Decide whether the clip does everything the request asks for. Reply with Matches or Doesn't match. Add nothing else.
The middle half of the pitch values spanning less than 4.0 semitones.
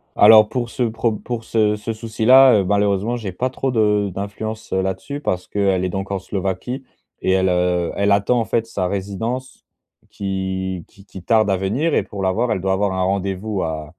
Matches